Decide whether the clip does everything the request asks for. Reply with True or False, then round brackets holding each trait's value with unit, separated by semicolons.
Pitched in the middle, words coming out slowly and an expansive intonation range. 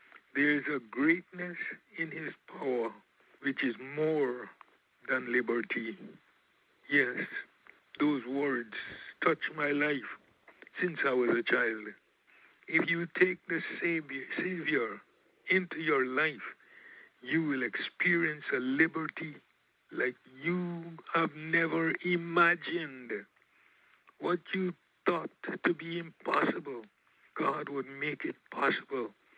False (165 Hz; 105 wpm; 3.1 semitones)